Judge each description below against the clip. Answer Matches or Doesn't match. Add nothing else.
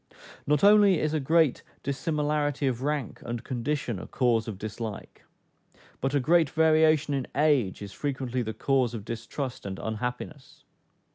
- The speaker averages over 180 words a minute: Doesn't match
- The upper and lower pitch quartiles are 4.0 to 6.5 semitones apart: Matches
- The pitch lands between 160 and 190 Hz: Doesn't match